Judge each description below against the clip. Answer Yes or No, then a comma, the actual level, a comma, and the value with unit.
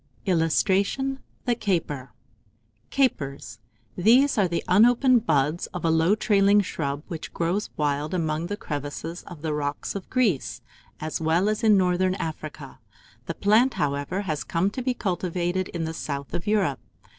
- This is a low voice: No, medium, 175 Hz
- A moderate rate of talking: Yes, average, 155 wpm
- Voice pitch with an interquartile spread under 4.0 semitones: No, average, 5.0 semitones